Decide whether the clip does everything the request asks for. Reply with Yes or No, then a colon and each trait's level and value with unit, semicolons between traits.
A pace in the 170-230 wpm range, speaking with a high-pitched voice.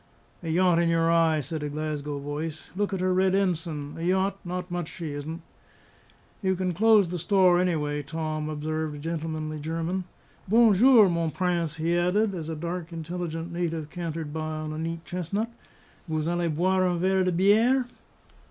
No: average, 180 wpm; medium, 170 Hz